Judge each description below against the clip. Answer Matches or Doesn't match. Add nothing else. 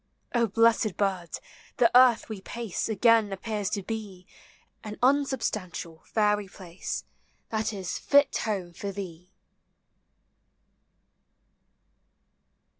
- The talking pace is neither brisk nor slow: Doesn't match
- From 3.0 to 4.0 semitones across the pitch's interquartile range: Matches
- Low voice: Doesn't match